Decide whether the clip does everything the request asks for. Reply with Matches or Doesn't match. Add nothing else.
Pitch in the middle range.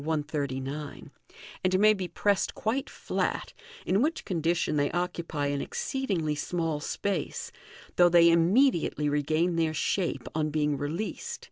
Matches